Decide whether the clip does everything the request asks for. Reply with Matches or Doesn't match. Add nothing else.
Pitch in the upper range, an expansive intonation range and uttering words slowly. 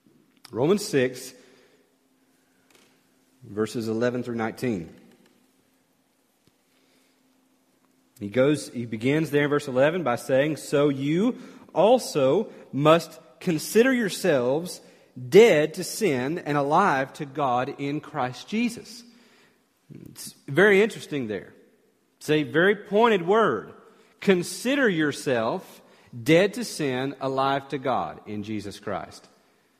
Doesn't match